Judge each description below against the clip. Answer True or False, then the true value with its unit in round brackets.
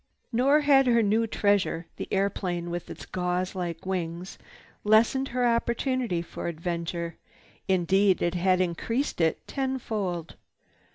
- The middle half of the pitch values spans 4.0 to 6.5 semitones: True (5.1 semitones)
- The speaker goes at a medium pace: False (125 wpm)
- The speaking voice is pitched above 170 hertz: True (190 Hz)